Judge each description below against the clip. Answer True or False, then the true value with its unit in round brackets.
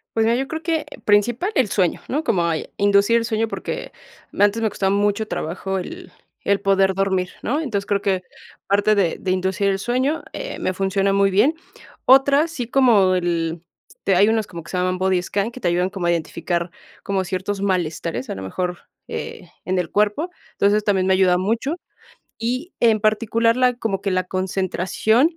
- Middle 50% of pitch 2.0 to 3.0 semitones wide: False (3.6 semitones)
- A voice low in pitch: False (200 Hz)